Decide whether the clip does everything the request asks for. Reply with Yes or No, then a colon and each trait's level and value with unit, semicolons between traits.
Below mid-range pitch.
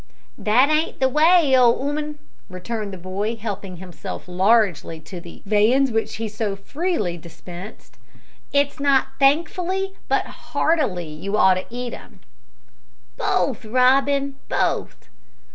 No: high, 235 Hz